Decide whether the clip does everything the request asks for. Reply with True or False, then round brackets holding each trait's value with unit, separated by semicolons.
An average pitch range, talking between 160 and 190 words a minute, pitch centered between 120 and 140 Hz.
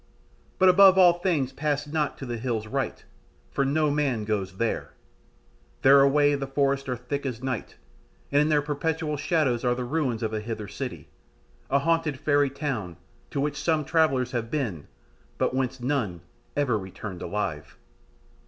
True (4.1 semitones; 165 wpm; 135 Hz)